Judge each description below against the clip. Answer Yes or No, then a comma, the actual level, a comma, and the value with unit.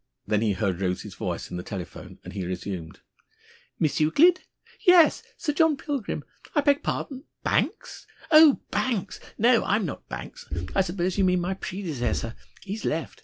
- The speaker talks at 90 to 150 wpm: No, average, 160 wpm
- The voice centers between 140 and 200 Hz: Yes, medium, 185 Hz